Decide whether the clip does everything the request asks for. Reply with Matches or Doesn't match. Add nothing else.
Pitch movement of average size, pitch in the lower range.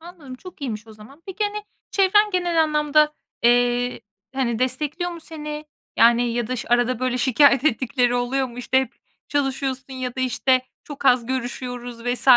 Doesn't match